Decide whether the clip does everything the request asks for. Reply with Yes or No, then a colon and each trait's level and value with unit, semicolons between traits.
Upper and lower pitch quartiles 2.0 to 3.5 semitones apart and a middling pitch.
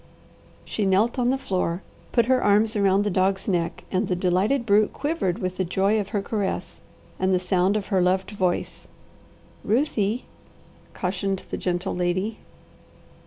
No: average, 2.7 semitones; high, 195 Hz